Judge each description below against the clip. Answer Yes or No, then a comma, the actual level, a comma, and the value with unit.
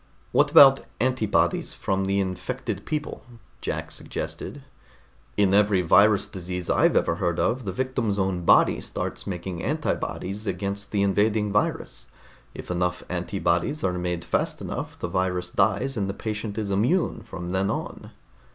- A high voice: No, low, 100 Hz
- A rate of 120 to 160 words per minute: Yes, average, 150 wpm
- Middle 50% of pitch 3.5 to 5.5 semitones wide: No, average, 2.9 semitones